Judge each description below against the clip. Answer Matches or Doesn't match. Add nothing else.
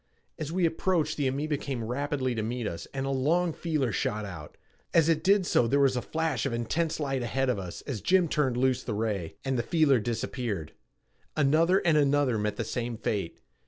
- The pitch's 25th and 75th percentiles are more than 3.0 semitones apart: Matches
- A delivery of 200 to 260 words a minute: Matches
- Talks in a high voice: Doesn't match